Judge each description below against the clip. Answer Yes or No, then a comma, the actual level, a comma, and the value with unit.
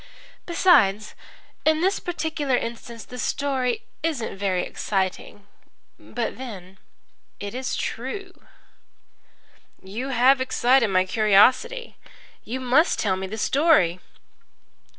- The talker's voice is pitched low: No, high, 245 Hz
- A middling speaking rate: No, slow, 100 wpm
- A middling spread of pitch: No, wide, 5.8 semitones